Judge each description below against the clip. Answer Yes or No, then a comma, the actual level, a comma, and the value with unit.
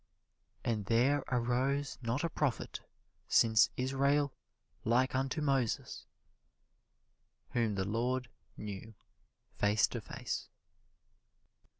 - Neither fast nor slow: No, slow, 90 wpm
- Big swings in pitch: No, average, 3.2 semitones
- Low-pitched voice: Yes, low, 125 Hz